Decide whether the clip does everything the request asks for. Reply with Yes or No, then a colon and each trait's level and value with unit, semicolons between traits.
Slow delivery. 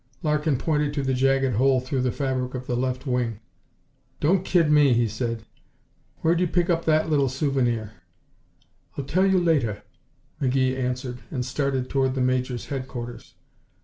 No: average, 160 wpm